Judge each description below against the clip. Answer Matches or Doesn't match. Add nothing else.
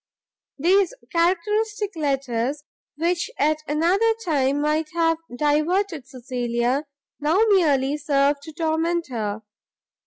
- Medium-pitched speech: Doesn't match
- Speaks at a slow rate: Matches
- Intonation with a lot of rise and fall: Doesn't match